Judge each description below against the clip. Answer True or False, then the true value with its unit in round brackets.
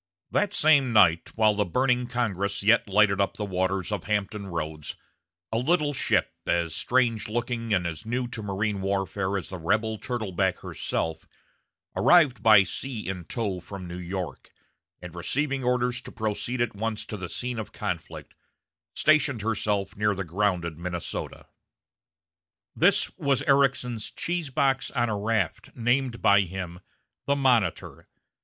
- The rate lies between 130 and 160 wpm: True (150 wpm)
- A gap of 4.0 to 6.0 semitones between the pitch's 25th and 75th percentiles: True (4.5 semitones)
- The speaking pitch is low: True (105 Hz)